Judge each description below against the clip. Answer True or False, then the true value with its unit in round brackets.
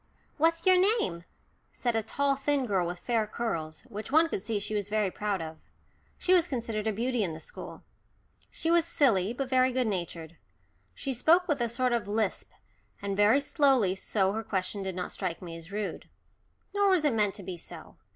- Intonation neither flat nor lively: False (6.0 semitones)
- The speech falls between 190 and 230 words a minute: True (200 wpm)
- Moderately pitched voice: False (220 Hz)